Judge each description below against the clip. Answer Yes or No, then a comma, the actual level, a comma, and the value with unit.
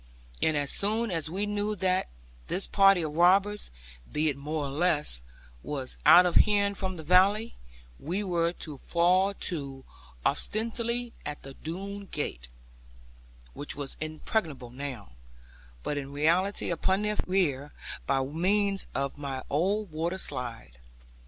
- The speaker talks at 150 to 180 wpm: No, average, 140 wpm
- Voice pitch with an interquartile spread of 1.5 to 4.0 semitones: No, wide, 5.5 semitones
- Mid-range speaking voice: Yes, medium, 170 Hz